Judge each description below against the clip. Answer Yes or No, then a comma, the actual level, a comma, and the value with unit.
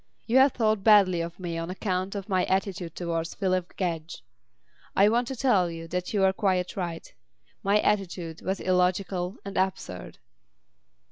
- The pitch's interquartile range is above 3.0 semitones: No, narrow, 2.5 semitones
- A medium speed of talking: Yes, average, 160 wpm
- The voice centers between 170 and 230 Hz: Yes, medium, 185 Hz